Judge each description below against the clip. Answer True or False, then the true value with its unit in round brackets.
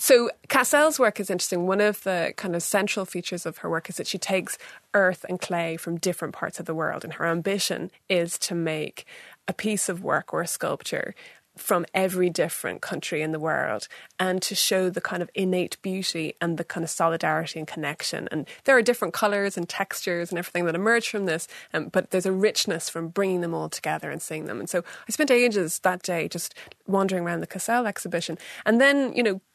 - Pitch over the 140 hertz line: True (185 Hz)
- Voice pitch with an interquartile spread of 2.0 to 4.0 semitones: True (3.0 semitones)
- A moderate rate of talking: False (215 wpm)